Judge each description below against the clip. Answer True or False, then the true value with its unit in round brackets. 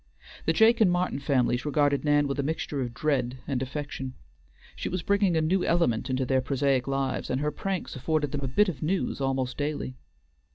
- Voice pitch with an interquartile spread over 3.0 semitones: True (3.4 semitones)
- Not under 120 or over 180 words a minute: False (200 wpm)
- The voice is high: False (145 Hz)